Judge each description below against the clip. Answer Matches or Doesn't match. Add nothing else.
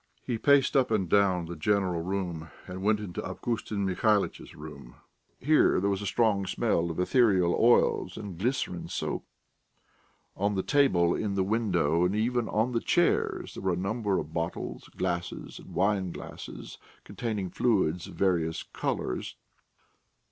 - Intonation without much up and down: Doesn't match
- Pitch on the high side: Doesn't match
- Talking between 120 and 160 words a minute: Matches